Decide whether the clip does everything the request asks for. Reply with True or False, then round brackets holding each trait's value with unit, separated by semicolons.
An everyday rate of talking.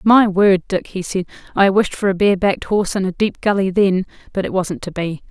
False (250 wpm)